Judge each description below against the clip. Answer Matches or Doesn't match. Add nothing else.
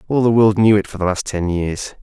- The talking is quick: Matches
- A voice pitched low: Matches